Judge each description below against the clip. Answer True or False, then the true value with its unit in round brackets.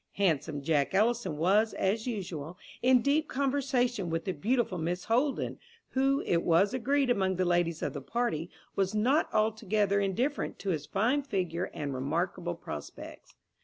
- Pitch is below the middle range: False (195 Hz)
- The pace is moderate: True (155 wpm)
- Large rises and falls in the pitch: True (6.3 semitones)